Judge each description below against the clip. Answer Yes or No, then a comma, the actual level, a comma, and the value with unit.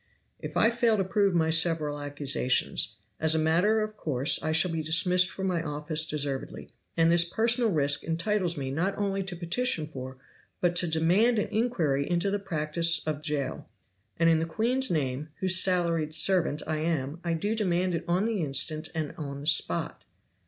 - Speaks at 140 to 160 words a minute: No, average, 185 wpm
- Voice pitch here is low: No, medium, 165 Hz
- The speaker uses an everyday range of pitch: Yes, average, 3.9 semitones